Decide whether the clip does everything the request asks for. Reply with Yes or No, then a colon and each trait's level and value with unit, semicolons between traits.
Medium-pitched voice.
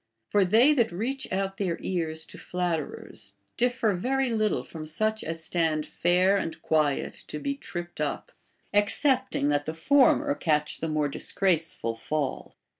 Yes: medium, 180 Hz